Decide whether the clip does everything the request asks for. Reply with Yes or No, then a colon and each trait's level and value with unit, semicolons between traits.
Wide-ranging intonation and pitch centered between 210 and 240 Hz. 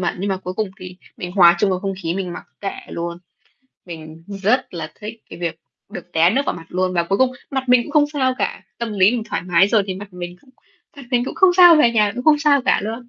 No: wide, 5.8 semitones; high, 195 Hz